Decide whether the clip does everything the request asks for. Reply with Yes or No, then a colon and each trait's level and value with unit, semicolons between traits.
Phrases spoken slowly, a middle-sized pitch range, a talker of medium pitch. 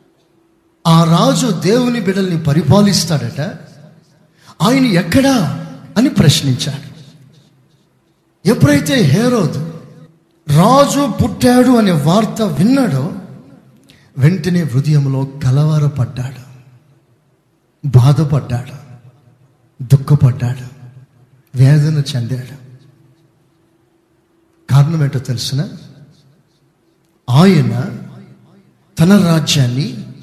Yes: slow, 60 wpm; average, 4.0 semitones; medium, 150 Hz